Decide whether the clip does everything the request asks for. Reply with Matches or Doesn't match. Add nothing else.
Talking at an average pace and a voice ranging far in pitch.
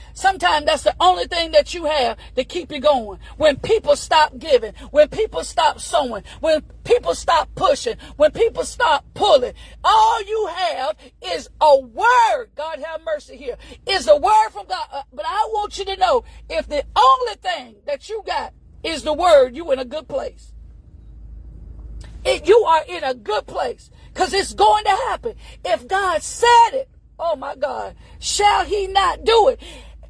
Matches